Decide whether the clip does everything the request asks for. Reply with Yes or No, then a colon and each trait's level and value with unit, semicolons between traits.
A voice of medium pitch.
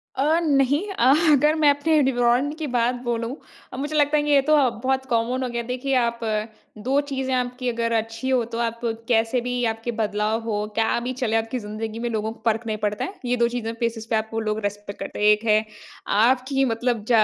No: high, 240 Hz